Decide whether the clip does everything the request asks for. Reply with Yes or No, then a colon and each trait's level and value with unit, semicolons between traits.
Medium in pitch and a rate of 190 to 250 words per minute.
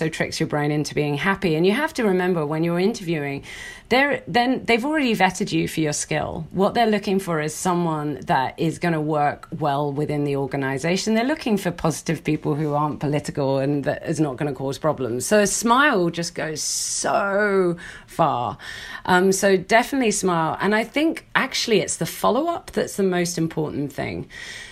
Yes: medium, 165 Hz; fast, 205 wpm